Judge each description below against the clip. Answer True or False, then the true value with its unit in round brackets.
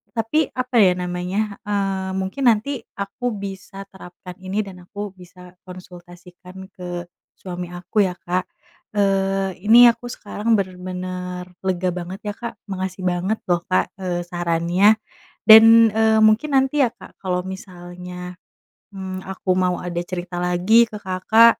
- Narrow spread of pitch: True (2.0 semitones)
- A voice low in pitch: False (185 Hz)